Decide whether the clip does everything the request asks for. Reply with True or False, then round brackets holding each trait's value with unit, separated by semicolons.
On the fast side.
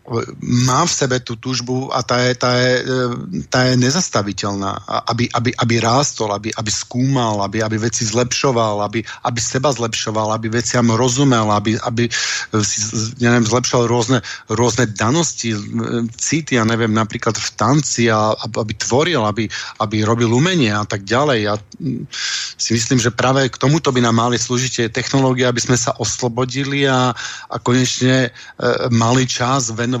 False (150 wpm)